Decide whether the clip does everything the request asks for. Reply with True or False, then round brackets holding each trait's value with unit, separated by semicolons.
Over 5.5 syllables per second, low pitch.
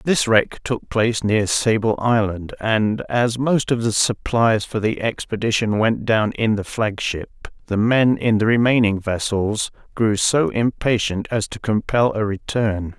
False (4.0 syllables/s; 110 Hz)